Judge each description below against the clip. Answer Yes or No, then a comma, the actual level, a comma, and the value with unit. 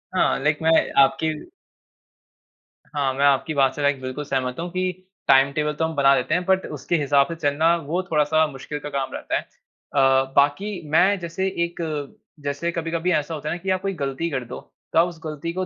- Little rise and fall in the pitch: No, average, 3.4 semitones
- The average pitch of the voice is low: No, medium, 150 Hz